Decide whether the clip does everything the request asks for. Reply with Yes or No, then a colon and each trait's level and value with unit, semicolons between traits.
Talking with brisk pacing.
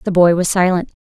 Yes: fast, 235 wpm